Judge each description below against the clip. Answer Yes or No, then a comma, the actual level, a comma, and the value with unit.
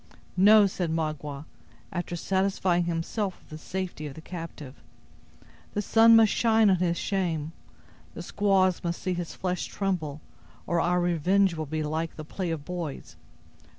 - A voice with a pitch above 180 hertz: No, medium, 175 Hz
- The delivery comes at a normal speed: Yes, average, 155 wpm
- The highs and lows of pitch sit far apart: No, average, 3.1 semitones